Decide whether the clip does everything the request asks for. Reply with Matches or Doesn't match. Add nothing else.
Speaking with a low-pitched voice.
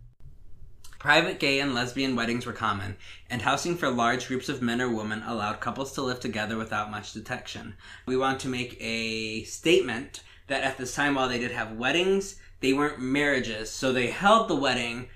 Matches